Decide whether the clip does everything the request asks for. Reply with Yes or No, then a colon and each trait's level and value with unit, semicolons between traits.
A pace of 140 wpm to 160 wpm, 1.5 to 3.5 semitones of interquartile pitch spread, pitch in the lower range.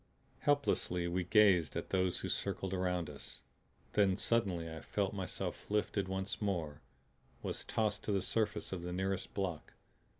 Yes: average, 155 wpm; average, 2.7 semitones; very low, 95 Hz